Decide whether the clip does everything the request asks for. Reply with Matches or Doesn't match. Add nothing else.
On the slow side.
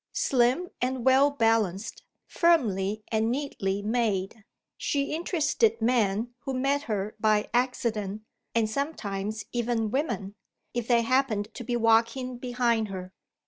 Matches